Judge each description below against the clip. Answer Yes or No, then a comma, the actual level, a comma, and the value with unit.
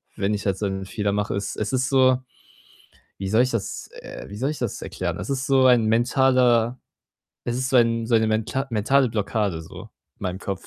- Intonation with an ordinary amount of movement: Yes, average, 4.0 semitones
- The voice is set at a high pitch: No, low, 115 Hz